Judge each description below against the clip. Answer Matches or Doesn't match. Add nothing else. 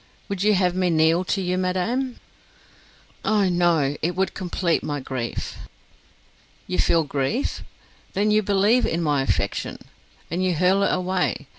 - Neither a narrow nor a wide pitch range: Matches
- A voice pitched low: Doesn't match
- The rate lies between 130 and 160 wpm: Matches